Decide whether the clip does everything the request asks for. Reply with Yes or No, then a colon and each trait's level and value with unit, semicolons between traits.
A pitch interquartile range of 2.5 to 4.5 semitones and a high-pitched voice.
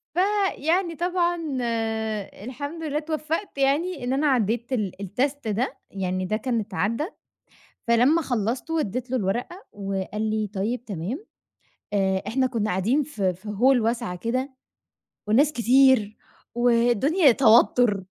No: wide, 5.5 semitones; high, 245 Hz